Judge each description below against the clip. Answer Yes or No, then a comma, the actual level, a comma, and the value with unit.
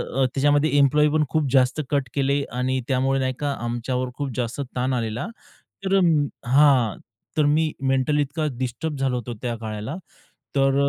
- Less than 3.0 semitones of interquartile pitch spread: Yes, narrow, 2.5 semitones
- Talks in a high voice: No, low, 135 Hz